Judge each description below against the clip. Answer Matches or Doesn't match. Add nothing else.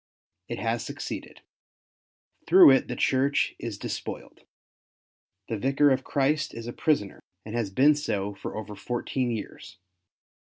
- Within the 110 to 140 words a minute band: Matches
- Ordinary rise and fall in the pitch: Matches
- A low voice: Matches